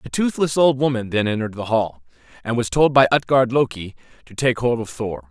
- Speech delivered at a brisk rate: Yes, fast, 215 wpm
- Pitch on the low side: Yes, low, 125 Hz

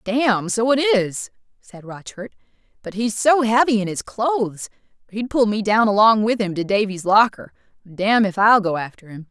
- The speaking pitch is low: No, high, 215 Hz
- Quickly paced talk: No, average, 180 wpm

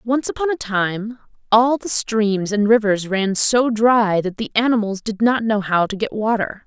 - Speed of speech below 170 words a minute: No, average, 200 wpm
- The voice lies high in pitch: Yes, high, 220 Hz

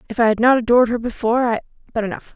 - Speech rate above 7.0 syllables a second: Yes, 8.2 syllables/s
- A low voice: No, high, 230 Hz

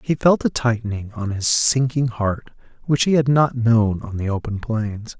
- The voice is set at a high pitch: No, low, 115 Hz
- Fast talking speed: No, average, 195 wpm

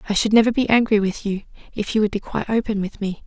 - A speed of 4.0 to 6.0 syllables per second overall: No, 6.8 syllables/s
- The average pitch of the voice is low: No, high, 210 Hz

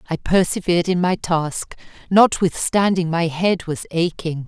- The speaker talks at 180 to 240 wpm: No, slow, 135 wpm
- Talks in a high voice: No, medium, 175 Hz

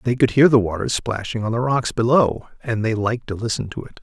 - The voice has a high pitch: No, low, 115 Hz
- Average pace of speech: No, fast, 255 wpm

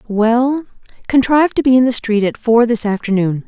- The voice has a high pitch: Yes, high, 235 Hz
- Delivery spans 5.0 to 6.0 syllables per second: Yes, 5.2 syllables/s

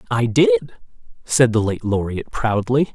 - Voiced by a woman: No, male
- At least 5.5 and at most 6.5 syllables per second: No, 4.5 syllables/s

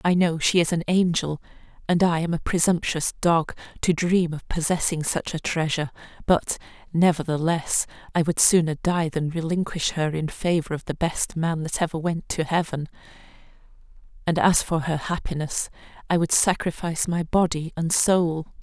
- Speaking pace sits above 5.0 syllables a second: No, 4.9 syllables/s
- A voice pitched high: No, medium, 165 Hz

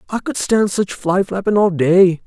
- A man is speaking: Yes, male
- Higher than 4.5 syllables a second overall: No, 4.4 syllables/s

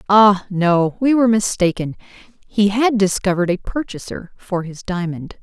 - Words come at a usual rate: Yes, average, 145 wpm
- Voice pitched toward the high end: Yes, high, 195 Hz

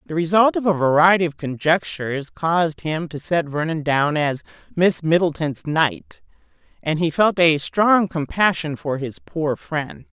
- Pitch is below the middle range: No, medium, 160 Hz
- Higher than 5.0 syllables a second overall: No, 4.4 syllables/s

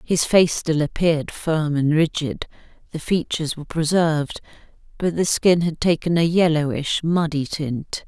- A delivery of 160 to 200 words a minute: No, average, 150 wpm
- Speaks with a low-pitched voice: No, medium, 160 Hz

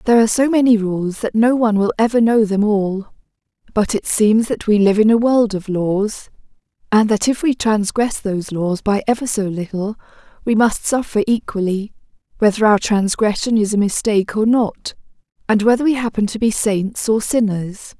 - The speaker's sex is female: Yes, female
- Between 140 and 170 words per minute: No, average, 185 wpm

